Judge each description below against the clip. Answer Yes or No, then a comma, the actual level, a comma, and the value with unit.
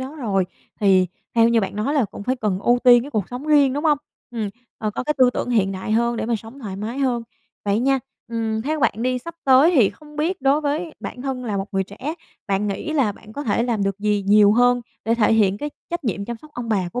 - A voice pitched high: Yes, high, 235 Hz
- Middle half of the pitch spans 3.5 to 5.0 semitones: Yes, average, 4.6 semitones